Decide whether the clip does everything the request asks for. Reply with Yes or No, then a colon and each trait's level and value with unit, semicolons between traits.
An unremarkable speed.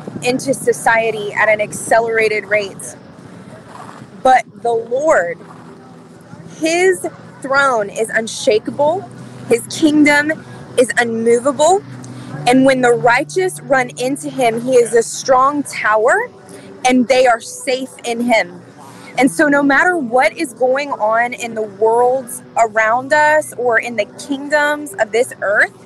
No: slow, 130 wpm